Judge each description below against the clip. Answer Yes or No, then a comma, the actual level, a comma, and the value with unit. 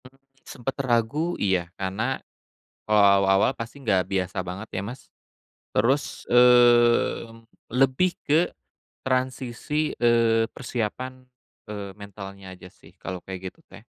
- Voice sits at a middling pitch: No, low, 115 Hz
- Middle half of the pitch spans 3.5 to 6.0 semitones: Yes, average, 4.7 semitones